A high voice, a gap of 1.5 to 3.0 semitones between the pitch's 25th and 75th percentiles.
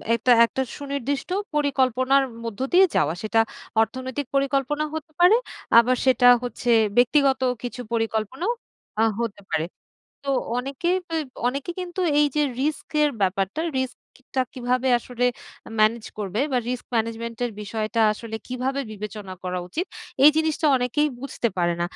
No: very high, 255 Hz; average, 3.8 semitones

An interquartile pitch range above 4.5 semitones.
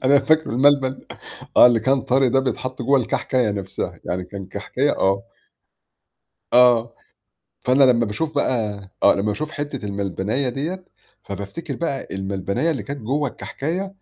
Yes: wide, 5.5 semitones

